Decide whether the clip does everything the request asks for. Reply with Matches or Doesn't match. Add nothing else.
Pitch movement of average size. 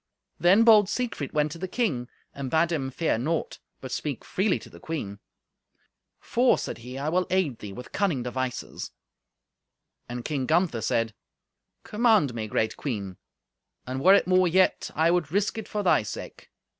Doesn't match